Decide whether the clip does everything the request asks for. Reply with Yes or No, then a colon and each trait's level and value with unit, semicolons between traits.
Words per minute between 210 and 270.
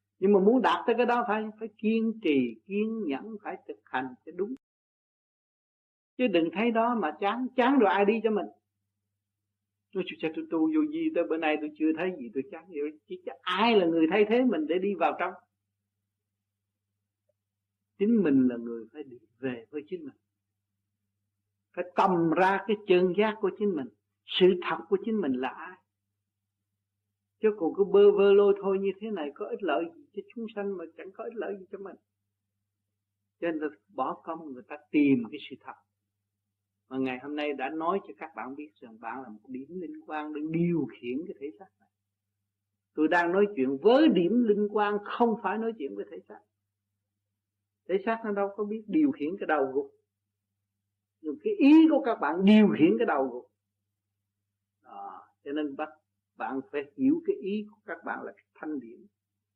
No: average, 200 wpm